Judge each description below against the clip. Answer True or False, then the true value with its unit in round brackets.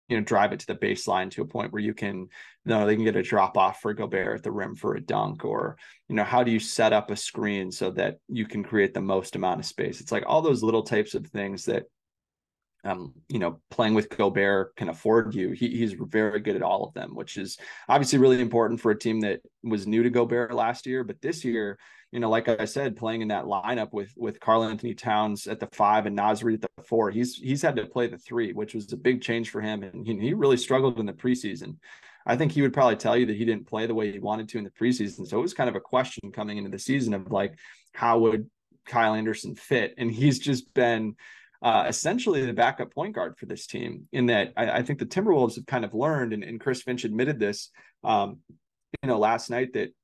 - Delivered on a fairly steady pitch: True (2.3 semitones)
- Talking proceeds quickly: True (250 wpm)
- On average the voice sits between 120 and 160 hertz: False (110 Hz)